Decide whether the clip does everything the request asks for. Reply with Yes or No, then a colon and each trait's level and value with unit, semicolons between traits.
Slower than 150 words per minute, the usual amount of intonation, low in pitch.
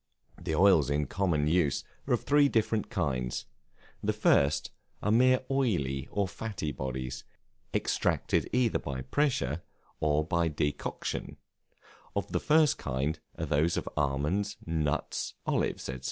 No: slow, 135 wpm; wide, 6.5 semitones; very low, 80 Hz